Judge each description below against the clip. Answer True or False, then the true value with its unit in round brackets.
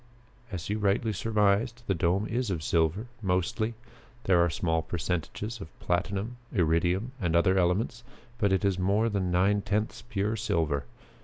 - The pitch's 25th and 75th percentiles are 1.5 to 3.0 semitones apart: False (3.6 semitones)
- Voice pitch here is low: True (95 Hz)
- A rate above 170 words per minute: False (155 wpm)